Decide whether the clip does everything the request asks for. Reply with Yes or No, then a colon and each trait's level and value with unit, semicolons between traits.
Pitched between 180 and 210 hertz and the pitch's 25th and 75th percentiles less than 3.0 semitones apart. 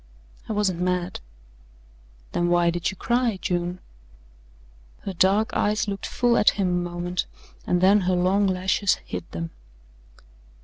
Yes: medium, 185 Hz; narrow, 2.4 semitones